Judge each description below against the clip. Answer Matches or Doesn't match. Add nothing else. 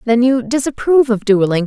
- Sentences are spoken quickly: Doesn't match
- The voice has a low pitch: Doesn't match